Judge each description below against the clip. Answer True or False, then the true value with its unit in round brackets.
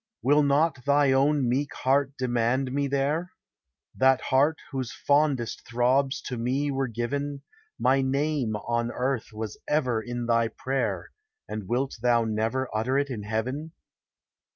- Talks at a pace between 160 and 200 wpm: False (145 wpm)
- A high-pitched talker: False (130 Hz)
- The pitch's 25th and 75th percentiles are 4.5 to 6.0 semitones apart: False (3.0 semitones)